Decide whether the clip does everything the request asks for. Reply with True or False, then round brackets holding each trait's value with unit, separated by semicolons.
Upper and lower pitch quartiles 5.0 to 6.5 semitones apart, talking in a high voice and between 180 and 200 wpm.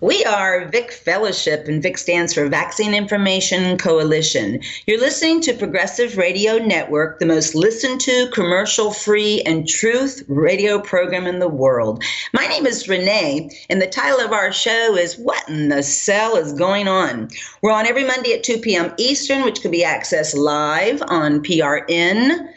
False (5.6 semitones; 195 Hz; 170 wpm)